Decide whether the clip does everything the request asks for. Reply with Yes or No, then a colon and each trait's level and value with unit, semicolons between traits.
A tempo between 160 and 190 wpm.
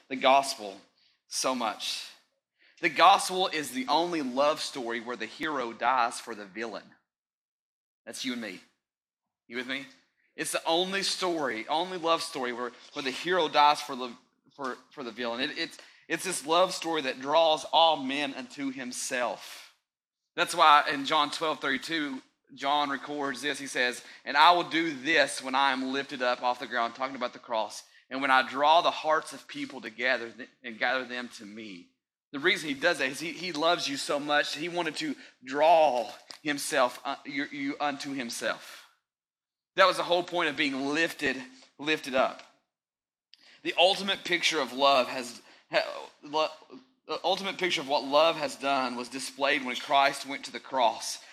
Yes: average, 180 wpm